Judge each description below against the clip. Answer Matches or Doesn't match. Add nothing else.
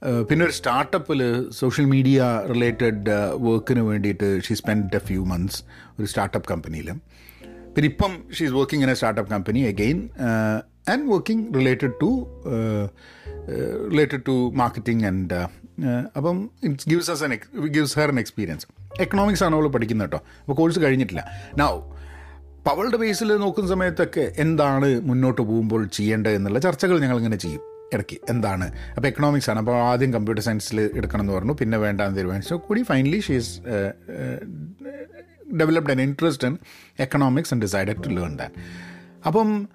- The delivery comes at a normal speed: Doesn't match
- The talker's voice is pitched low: Matches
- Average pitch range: Doesn't match